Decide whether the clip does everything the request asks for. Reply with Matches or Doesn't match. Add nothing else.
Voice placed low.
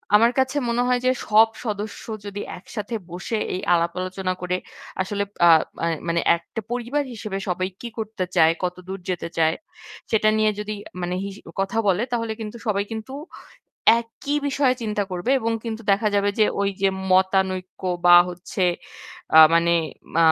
Doesn't match